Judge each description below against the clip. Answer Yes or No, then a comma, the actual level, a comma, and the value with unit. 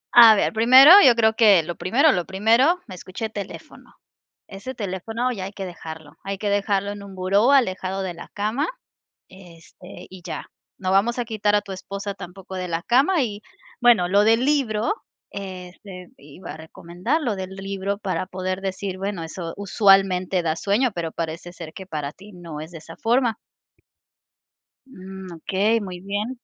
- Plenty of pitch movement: No, average, 3.3 semitones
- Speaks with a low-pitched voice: No, high, 195 Hz